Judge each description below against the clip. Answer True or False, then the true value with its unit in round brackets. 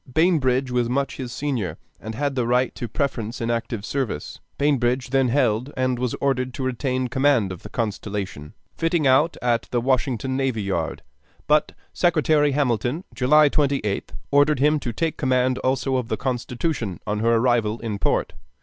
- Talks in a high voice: False (130 Hz)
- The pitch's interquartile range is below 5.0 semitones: True (3.2 semitones)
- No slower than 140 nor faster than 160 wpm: False (170 wpm)